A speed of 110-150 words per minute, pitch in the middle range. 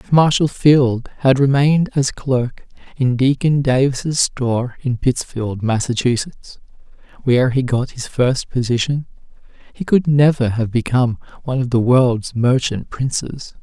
No: slow, 135 wpm; low, 130 Hz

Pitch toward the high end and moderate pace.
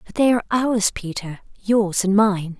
Yes: high, 205 Hz; average, 185 wpm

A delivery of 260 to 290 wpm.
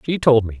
No: fast, 300 wpm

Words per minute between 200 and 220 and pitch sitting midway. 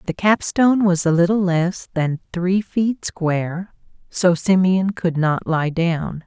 No: average, 155 wpm; medium, 180 Hz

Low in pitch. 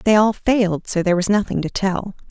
No: high, 200 Hz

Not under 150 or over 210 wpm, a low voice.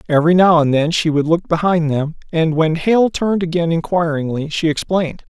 No: average, 190 wpm; medium, 165 Hz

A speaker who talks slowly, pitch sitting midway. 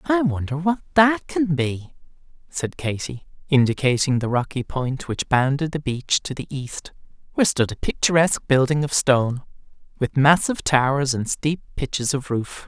No: average, 160 wpm; medium, 145 Hz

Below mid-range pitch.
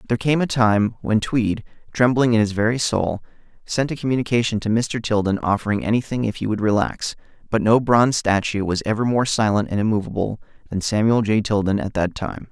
Yes: low, 110 Hz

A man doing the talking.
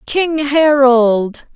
No: female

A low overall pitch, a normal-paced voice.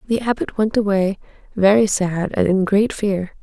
No: high, 200 Hz; average, 175 wpm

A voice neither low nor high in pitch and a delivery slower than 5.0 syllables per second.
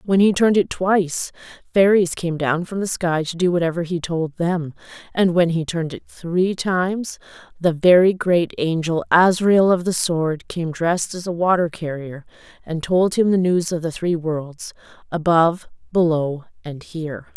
Yes: medium, 170 Hz; 4.6 syllables/s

